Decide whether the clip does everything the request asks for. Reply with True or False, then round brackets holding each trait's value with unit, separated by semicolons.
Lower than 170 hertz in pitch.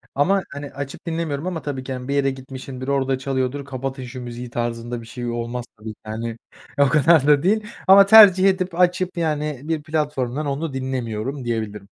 True (135 Hz)